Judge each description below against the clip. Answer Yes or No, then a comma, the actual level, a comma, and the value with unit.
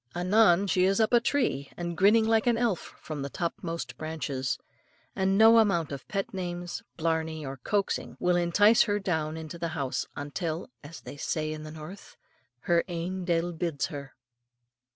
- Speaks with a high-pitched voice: No, medium, 170 Hz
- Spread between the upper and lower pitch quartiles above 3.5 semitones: Yes, average, 4.0 semitones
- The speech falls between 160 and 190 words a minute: Yes, average, 175 wpm